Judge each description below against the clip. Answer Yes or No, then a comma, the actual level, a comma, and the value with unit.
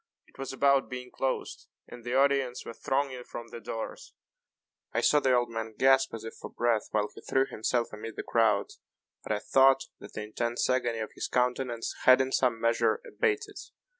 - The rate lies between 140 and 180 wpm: No, average, 195 wpm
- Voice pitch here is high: No, low, 125 Hz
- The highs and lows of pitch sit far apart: No, narrow, 2.6 semitones